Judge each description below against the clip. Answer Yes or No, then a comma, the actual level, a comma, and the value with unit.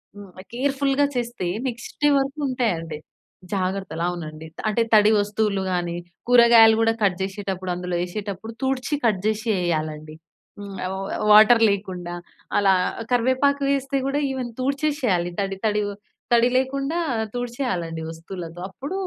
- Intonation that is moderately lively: No, wide, 5.8 semitones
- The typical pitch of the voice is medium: No, high, 210 Hz